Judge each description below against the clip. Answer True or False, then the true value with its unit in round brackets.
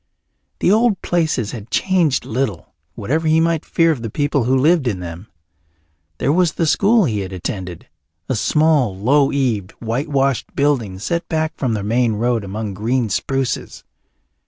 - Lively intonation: True (6.6 semitones)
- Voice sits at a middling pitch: False (130 Hz)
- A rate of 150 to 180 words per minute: True (165 wpm)